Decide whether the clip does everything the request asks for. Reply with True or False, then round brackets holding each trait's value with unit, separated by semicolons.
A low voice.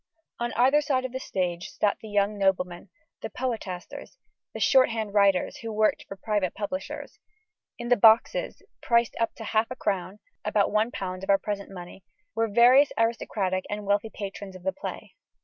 False (210 Hz)